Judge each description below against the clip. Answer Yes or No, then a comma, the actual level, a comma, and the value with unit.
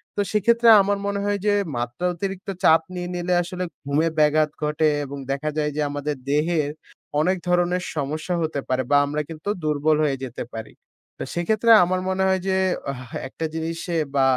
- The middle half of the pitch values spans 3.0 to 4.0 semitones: Yes, average, 3.7 semitones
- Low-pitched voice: No, medium, 160 Hz